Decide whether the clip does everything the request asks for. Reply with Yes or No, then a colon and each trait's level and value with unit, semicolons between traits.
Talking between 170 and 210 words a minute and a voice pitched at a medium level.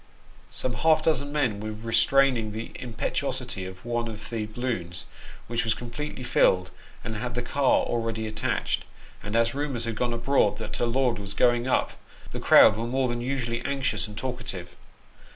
No: average, 175 wpm; low, 115 Hz